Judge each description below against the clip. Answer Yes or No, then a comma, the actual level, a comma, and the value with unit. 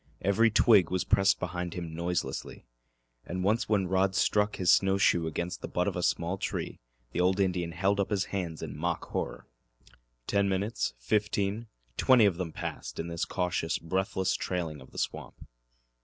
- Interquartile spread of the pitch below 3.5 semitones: Yes, average, 2.7 semitones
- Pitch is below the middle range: Yes, very low, 95 Hz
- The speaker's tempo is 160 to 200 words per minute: Yes, average, 175 wpm